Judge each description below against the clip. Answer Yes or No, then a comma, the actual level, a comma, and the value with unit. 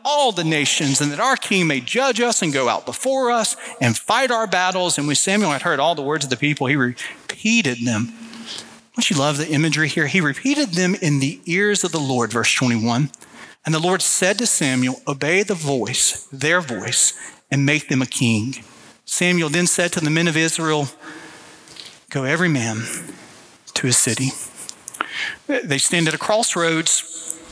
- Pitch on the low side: No, medium, 160 Hz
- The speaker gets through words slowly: No, average, 185 wpm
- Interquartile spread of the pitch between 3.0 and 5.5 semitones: Yes, average, 5.0 semitones